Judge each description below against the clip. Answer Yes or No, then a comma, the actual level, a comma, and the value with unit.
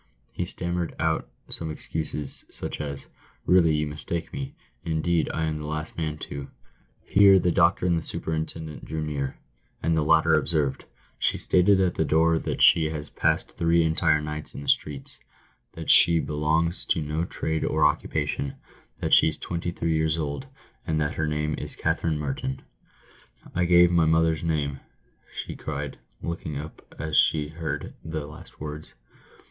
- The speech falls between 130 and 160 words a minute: No, average, 175 wpm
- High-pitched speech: No, very low, 80 Hz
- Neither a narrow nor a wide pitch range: No, narrow, 1.7 semitones